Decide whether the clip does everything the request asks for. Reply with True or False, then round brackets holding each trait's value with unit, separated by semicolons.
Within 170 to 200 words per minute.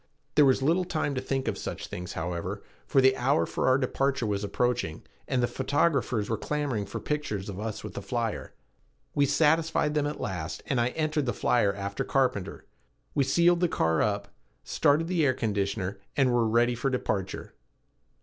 True (185 wpm)